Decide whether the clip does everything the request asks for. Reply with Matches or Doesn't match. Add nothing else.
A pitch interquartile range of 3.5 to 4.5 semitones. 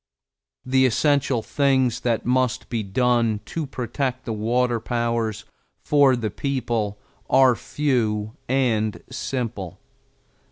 Doesn't match